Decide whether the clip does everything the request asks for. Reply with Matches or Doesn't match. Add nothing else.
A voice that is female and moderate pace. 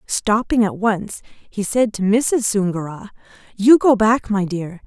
Matches